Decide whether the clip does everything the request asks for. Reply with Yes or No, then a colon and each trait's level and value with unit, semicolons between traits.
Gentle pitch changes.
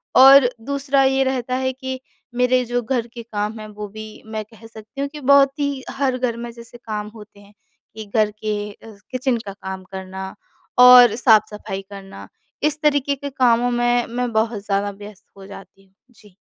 No: average, 3.7 semitones